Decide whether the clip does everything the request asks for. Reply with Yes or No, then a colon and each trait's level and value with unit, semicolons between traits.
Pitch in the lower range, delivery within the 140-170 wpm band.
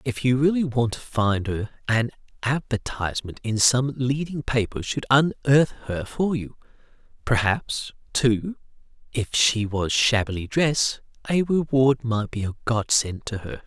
Yes: low, 120 Hz; average, 150 wpm